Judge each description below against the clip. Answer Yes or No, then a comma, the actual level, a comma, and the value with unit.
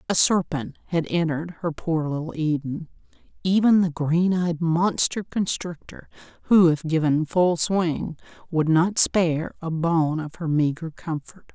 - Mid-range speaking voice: Yes, medium, 165 Hz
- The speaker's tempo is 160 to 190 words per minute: No, average, 140 wpm